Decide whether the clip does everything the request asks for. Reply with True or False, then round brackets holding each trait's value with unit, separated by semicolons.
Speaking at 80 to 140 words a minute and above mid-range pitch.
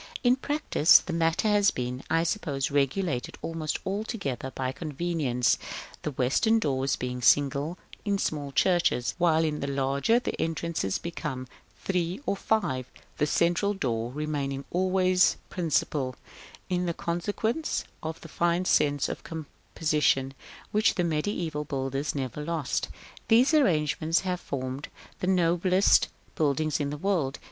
False (135 wpm; 160 Hz)